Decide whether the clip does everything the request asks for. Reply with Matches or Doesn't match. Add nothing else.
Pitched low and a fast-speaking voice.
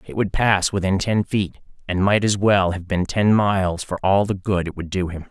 Matches